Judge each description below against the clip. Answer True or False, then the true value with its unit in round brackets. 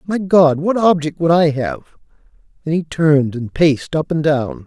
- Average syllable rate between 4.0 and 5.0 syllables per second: True (4.9 syllables/s)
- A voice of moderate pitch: True (160 Hz)